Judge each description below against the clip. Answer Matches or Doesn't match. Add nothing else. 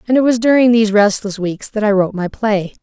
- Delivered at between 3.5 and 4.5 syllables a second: Doesn't match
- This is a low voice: Doesn't match